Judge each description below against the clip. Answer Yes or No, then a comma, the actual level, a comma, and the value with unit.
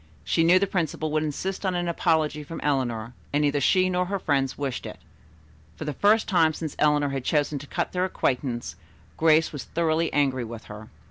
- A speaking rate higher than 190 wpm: Yes, average, 200 wpm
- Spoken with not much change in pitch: No, average, 3.7 semitones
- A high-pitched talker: No, medium, 150 Hz